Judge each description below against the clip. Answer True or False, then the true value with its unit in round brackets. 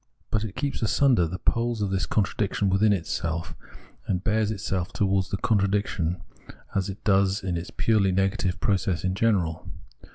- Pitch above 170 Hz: False (95 Hz)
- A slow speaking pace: False (160 wpm)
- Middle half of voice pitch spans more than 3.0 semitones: False (2.7 semitones)